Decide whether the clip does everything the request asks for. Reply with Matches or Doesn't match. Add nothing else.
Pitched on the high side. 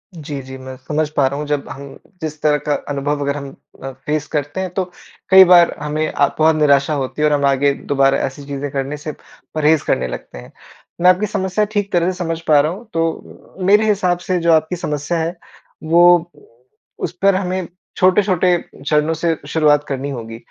Doesn't match